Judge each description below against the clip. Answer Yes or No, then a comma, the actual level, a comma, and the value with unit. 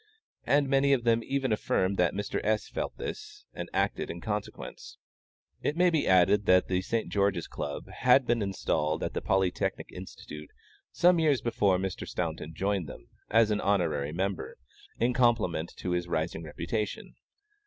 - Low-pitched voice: Yes, low, 100 Hz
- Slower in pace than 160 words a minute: No, average, 165 wpm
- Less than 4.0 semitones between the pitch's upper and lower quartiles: No, average, 5.2 semitones